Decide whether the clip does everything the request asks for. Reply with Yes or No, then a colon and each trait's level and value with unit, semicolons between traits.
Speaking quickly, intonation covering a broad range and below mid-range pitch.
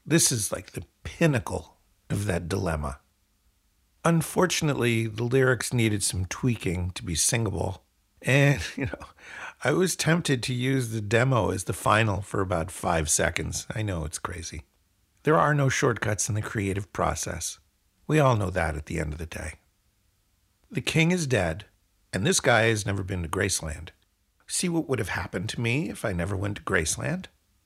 No: average, 175 wpm; wide, 5.8 semitones; low, 100 Hz